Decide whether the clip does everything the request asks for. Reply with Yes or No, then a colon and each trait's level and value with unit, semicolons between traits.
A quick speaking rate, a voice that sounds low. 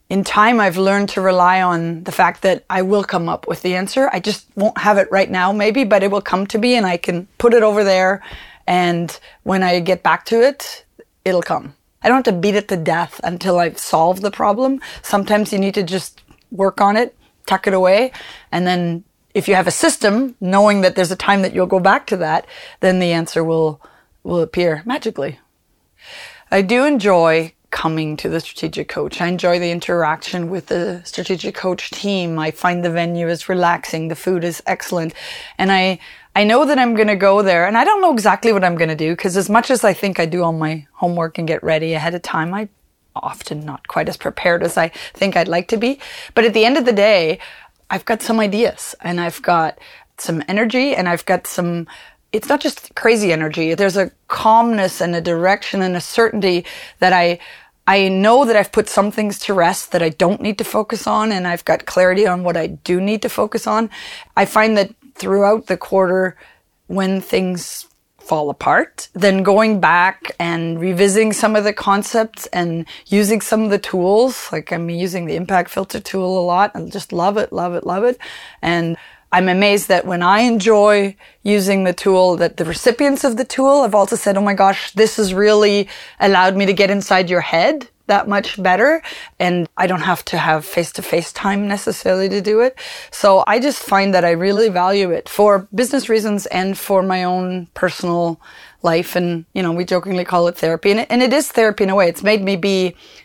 No: fast, 210 wpm; high, 195 Hz